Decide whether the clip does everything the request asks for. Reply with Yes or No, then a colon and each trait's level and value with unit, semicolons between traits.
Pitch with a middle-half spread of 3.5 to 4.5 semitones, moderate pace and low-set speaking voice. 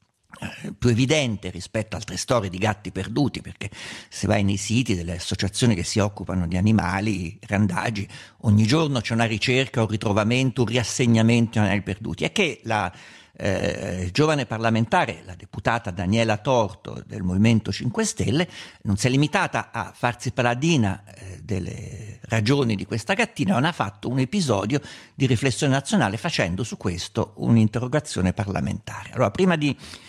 Yes: average, 4.2 semitones; average, 150 wpm; low, 110 Hz